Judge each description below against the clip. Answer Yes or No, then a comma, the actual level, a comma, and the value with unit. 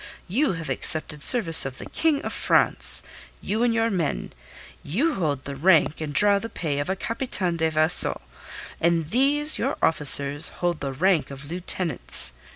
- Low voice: No, medium, 170 Hz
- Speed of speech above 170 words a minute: No, average, 165 wpm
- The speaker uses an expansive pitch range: Yes, wide, 6.5 semitones